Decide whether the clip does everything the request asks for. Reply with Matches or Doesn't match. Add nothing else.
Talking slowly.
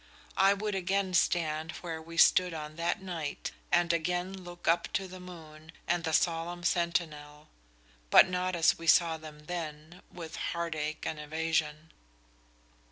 Doesn't match